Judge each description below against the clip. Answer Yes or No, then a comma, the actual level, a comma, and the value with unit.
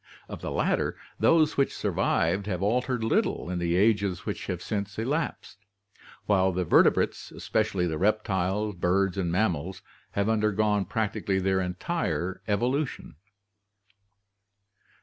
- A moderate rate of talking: No, slow, 125 wpm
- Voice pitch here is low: Yes, low, 100 Hz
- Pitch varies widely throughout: No, average, 2.8 semitones